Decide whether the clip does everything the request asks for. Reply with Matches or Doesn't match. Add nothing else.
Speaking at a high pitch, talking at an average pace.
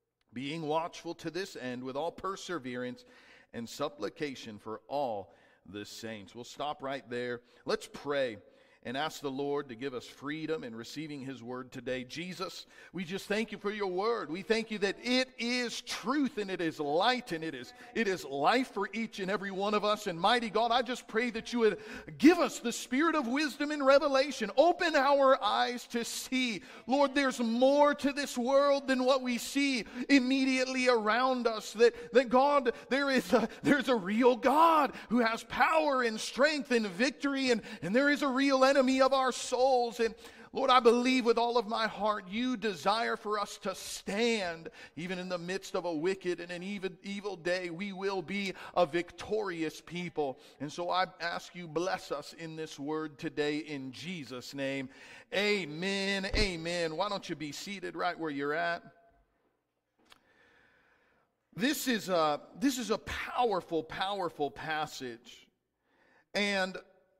Matches